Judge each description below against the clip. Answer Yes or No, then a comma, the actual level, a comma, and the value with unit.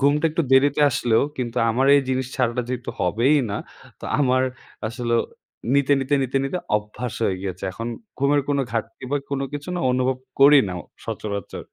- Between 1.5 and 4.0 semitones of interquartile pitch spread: Yes, average, 3.4 semitones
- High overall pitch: No, low, 130 Hz